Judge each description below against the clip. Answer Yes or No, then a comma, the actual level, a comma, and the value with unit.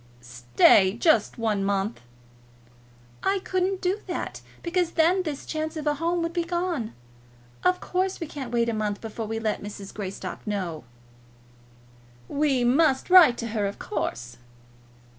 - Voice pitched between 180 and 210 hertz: No, very high, 260 Hz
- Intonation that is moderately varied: No, wide, 8.6 semitones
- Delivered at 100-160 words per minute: Yes, average, 150 wpm